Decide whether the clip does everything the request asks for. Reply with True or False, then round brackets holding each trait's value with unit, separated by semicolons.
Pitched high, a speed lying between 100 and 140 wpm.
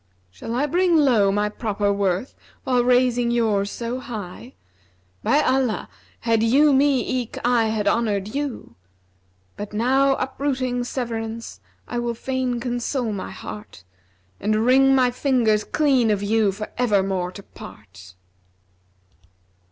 True (235 Hz; 135 wpm)